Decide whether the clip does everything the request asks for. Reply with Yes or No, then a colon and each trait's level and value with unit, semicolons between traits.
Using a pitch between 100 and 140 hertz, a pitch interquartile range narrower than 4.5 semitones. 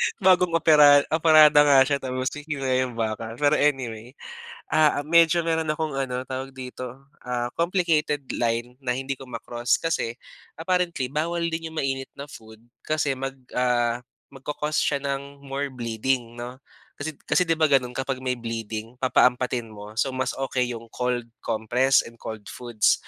Yes: low, 135 Hz; average, 3.5 semitones